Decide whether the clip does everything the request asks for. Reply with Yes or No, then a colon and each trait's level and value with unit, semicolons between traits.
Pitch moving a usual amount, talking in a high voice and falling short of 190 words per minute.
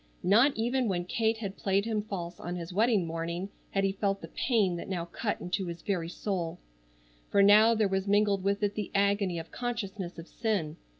No: average, 3.2 semitones; high, 195 Hz; average, 200 wpm